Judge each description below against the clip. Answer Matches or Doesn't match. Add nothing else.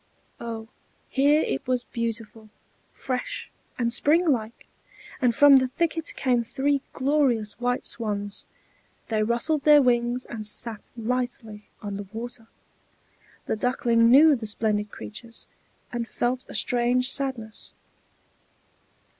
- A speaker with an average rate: Doesn't match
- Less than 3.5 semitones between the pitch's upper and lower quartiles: Matches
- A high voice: Matches